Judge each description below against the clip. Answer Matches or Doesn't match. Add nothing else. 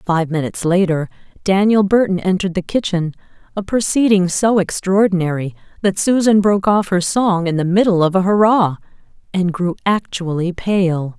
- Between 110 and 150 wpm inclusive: Matches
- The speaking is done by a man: Doesn't match